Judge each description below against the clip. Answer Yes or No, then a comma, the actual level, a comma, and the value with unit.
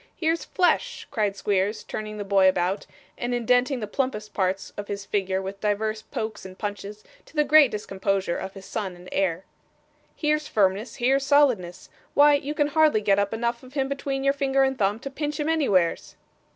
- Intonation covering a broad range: Yes, wide, 5.8 semitones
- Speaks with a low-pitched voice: No, high, 215 Hz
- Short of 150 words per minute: No, average, 190 wpm